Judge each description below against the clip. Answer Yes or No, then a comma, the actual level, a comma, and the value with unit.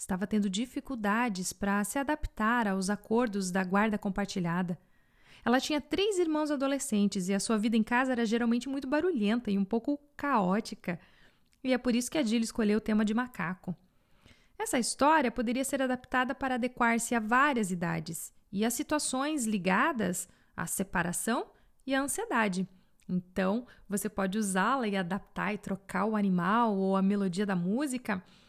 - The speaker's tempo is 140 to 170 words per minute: Yes, average, 160 wpm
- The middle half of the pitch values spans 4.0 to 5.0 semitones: Yes, average, 4.7 semitones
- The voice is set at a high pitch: Yes, high, 220 Hz